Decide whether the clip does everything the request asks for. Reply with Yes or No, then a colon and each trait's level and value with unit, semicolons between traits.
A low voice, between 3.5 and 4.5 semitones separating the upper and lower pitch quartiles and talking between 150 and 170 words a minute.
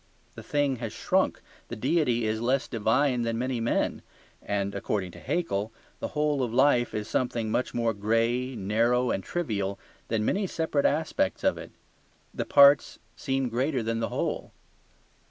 Yes: low, 120 Hz; average, 3.8 semitones; average, 160 wpm